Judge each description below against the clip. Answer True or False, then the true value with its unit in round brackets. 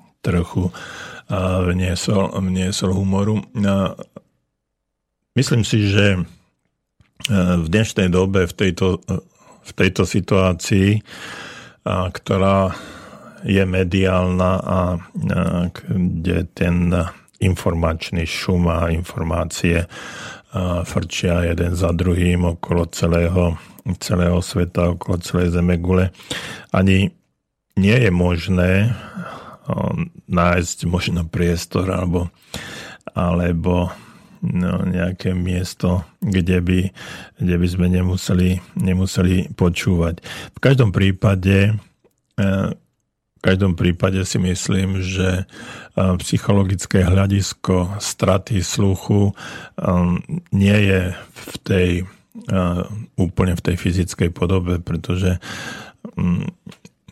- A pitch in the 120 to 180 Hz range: False (90 Hz)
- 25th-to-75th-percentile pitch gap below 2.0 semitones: True (1.6 semitones)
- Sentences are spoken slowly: True (85 wpm)